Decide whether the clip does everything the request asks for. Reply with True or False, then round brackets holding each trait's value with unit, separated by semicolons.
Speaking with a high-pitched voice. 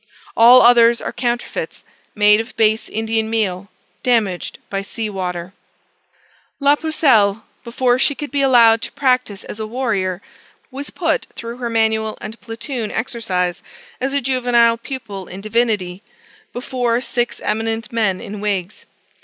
True (225 Hz)